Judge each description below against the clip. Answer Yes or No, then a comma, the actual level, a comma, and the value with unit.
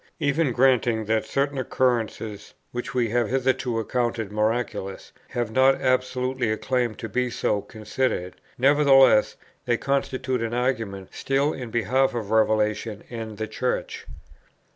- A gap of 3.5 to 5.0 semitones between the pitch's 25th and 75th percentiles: No, average, 3.1 semitones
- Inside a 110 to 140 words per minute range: Yes, slow, 135 wpm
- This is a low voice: Yes, low, 120 Hz